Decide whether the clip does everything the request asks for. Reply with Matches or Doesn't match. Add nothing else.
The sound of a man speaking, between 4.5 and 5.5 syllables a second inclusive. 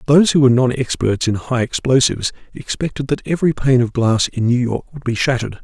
Doesn't match